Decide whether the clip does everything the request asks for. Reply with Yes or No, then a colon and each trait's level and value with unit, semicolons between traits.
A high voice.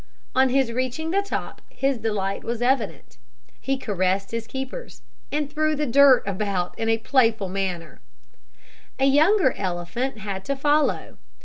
Yes: high, 240 Hz